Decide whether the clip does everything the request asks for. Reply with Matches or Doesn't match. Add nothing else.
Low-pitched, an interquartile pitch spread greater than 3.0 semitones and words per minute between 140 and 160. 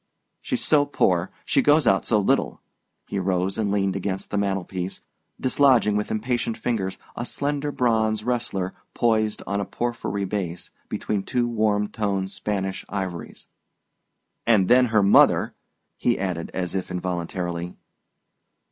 Matches